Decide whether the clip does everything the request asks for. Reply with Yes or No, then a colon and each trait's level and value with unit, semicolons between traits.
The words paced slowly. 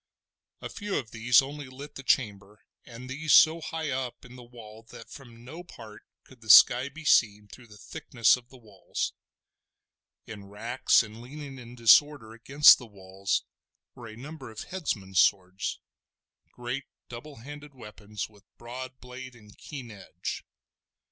No: average, 160 wpm